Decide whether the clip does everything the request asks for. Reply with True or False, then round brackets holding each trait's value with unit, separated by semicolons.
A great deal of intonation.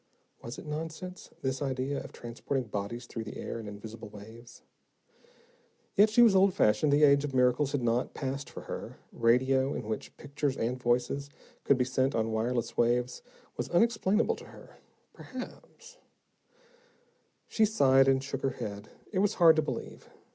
False (4.1 semitones)